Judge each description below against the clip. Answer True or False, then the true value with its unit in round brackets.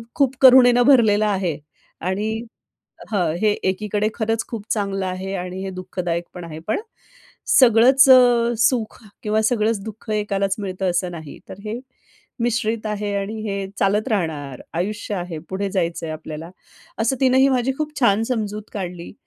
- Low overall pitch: False (210 Hz)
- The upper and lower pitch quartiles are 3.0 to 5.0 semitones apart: True (3.7 semitones)